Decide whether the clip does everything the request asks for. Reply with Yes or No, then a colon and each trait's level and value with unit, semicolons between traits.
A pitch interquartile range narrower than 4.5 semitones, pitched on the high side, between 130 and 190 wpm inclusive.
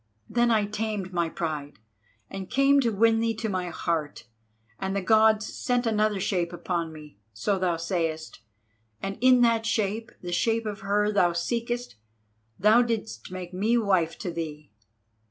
No: average, 4.9 semitones; high, 195 Hz; average, 155 wpm